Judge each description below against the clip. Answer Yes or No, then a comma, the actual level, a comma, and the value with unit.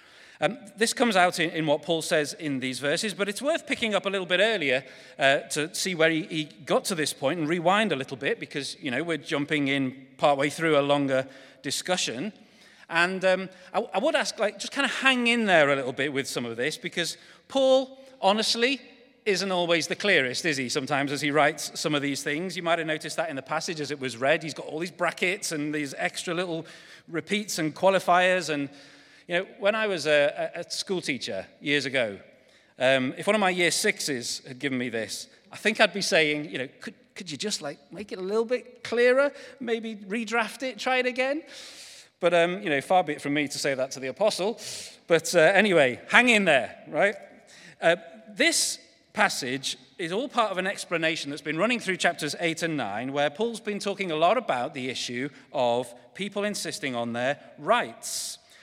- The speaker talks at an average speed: No, fast, 215 wpm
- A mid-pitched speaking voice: Yes, medium, 170 Hz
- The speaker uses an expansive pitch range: Yes, wide, 6.3 semitones